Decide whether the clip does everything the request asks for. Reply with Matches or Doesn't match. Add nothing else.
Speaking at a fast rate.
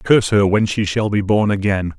Matches